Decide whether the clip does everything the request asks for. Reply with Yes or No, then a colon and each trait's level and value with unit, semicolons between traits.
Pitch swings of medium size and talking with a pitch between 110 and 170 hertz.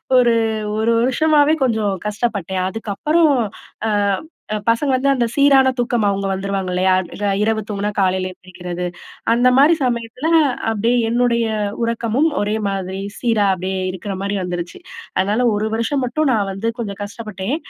No: average, 4.0 semitones; high, 220 Hz